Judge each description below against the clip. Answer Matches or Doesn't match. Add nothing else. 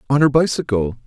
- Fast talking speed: Doesn't match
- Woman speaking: Doesn't match